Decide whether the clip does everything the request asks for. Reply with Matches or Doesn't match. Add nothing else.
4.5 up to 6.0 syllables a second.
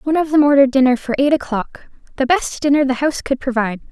Doesn't match